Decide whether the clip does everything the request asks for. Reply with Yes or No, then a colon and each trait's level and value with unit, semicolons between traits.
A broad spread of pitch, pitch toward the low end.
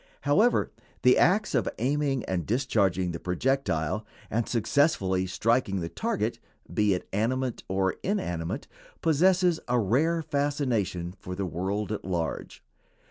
Yes: wide, 7.3 semitones; low, 110 Hz